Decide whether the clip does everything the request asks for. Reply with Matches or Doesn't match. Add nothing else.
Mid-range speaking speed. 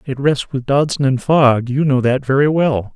Doesn't match